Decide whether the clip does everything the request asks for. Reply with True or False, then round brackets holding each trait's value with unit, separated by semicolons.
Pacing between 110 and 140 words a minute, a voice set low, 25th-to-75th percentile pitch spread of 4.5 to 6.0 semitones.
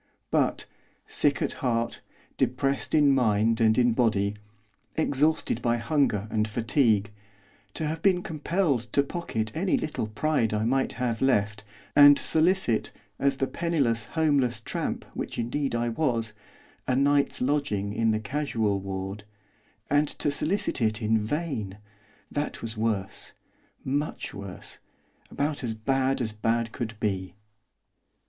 True (135 wpm; 120 Hz; 4.8 semitones)